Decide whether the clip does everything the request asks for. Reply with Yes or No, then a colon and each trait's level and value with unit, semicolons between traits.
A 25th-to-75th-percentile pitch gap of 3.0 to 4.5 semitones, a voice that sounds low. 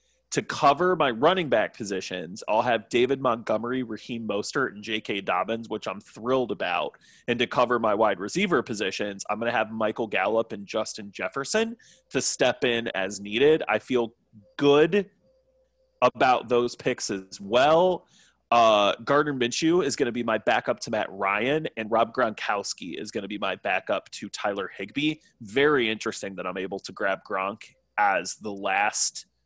No: wide, 5.6 semitones; low, 120 Hz